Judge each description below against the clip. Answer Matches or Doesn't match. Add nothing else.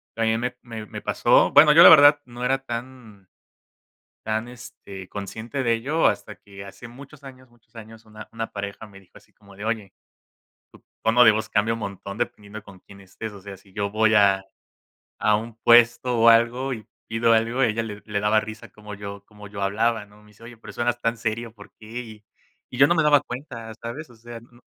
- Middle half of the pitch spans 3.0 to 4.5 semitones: Doesn't match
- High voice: Doesn't match